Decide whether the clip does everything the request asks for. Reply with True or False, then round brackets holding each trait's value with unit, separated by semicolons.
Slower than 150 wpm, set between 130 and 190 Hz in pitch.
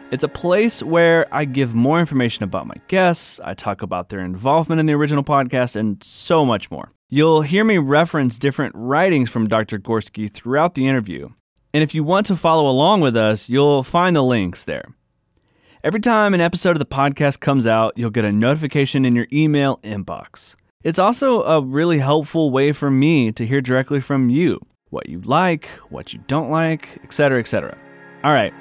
False (195 wpm; 140 Hz)